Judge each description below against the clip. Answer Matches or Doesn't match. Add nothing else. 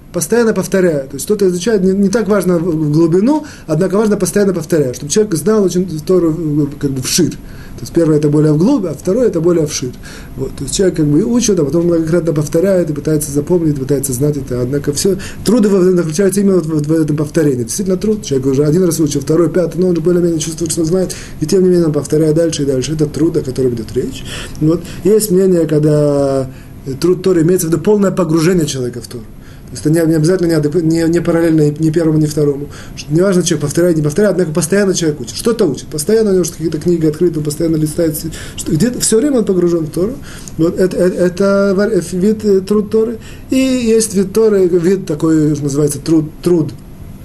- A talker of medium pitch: Matches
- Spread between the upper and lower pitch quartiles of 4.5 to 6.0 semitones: Doesn't match